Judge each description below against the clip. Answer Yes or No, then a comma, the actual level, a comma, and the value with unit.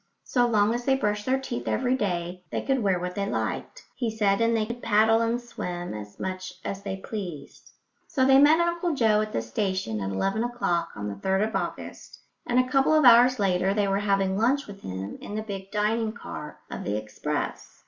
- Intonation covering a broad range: No, average, 4.4 semitones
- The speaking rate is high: Yes, fast, 215 wpm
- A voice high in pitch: Yes, high, 210 Hz